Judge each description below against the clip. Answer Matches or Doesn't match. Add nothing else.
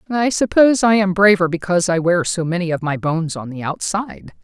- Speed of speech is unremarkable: Doesn't match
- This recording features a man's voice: Doesn't match